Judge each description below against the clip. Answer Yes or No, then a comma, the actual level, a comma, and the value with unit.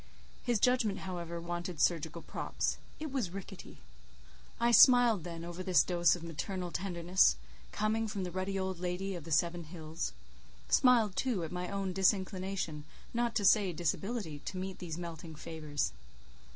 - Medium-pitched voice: Yes, medium, 180 Hz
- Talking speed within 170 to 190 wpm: No, average, 155 wpm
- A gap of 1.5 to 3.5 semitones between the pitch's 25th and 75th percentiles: Yes, average, 2.9 semitones